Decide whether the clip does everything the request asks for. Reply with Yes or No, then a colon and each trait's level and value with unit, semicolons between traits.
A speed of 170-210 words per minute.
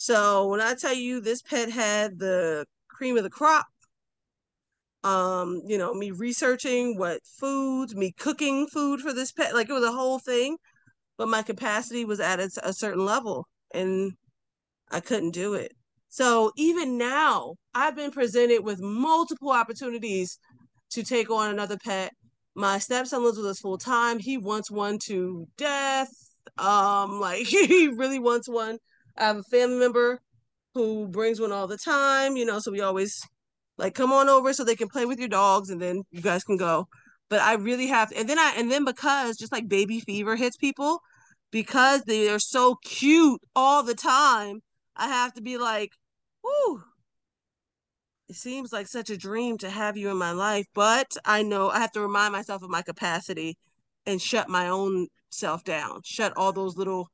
Yes: average, 185 wpm